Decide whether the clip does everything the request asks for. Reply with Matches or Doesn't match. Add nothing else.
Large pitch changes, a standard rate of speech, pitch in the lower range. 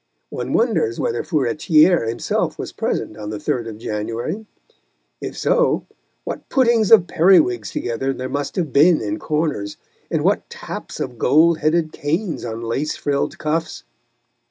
Doesn't match